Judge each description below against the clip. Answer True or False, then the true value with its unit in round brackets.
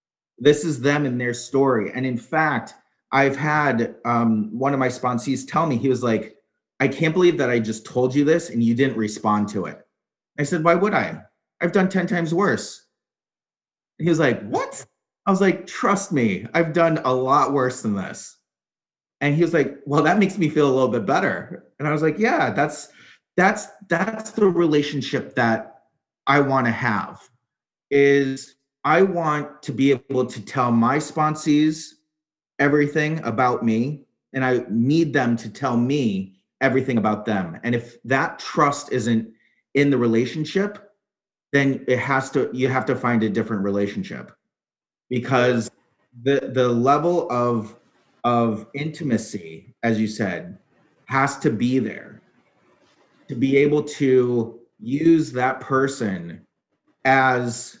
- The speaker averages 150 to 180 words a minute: True (160 wpm)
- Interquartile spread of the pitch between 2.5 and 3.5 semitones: False (4.4 semitones)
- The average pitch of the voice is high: False (135 Hz)